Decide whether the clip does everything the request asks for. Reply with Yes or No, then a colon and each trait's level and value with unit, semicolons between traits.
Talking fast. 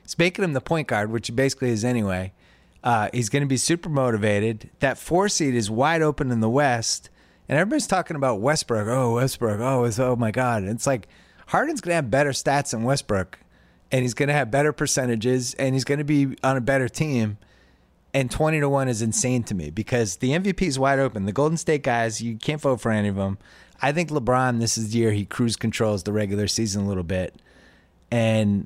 Yes: fast, 220 wpm